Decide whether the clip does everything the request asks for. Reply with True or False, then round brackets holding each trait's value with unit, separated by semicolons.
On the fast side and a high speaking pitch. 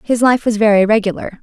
True (210 wpm; 215 Hz)